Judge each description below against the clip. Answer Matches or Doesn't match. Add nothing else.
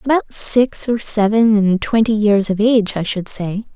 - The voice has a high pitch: Matches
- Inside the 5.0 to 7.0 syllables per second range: Doesn't match